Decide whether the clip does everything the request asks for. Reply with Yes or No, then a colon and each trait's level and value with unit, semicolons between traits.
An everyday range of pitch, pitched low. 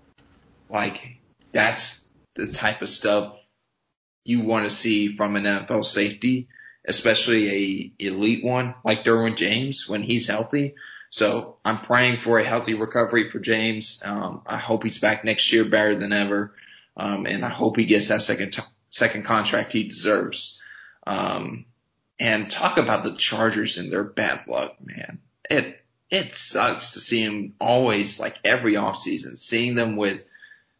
No: narrow, 2.0 semitones; low, 110 Hz